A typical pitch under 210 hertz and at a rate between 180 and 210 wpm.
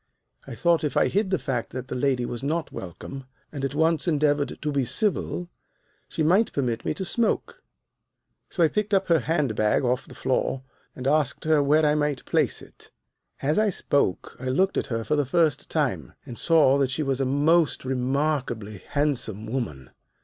Yes: medium, 140 Hz; average, 190 wpm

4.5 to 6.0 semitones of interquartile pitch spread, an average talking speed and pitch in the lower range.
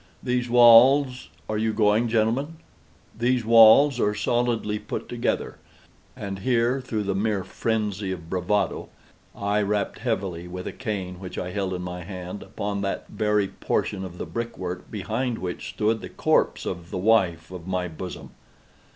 No: average, 3.9 semitones; average, 155 wpm; low, 105 Hz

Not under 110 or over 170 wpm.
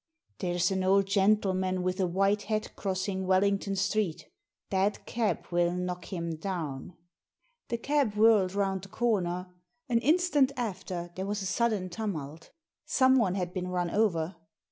Yes: average, 160 wpm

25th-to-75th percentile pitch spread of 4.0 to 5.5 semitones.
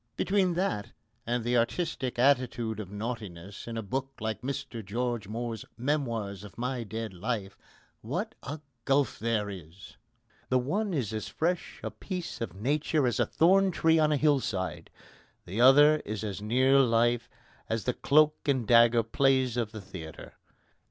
Yes: average, 4.5 semitones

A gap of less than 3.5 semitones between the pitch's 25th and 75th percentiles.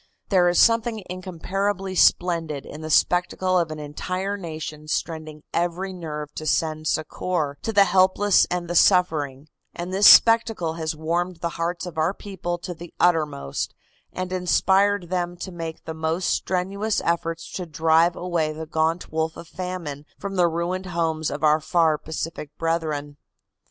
Yes: narrow, 2.6 semitones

